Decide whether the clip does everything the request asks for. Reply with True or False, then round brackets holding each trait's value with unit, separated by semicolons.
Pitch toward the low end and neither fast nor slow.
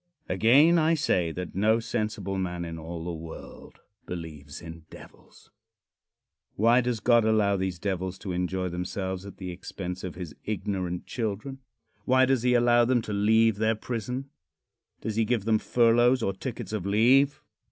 True (105 Hz; 165 wpm)